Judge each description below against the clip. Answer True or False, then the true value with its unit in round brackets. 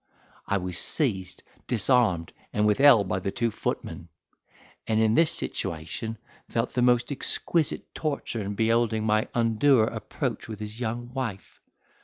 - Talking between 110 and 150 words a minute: True (135 wpm)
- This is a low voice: True (110 Hz)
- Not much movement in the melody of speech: False (3.0 semitones)